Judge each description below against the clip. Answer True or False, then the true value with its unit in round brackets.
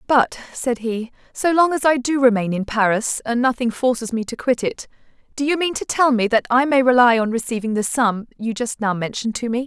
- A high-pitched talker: True (240 Hz)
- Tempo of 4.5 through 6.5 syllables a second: True (5.4 syllables/s)